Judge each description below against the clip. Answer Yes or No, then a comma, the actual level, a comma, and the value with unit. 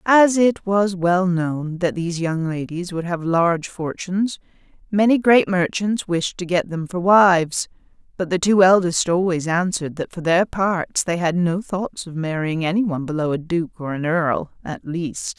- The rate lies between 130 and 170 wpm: No, average, 185 wpm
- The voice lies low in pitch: No, medium, 175 Hz